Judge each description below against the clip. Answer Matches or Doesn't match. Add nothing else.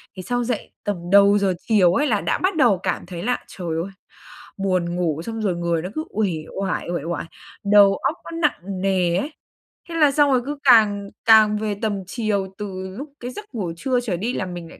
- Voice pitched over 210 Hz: Doesn't match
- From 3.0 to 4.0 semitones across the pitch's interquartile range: Doesn't match